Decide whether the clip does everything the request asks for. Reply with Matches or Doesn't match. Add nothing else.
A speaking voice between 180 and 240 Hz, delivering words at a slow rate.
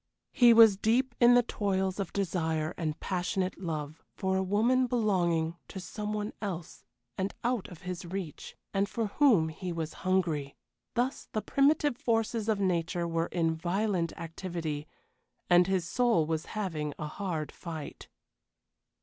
Doesn't match